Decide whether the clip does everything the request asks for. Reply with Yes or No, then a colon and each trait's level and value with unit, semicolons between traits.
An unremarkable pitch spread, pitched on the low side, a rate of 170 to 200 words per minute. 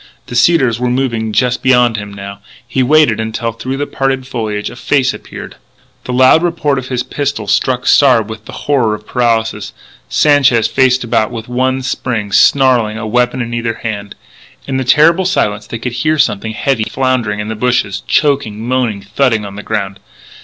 Yes: average, 3.2 semitones; low, 120 Hz; average, 180 wpm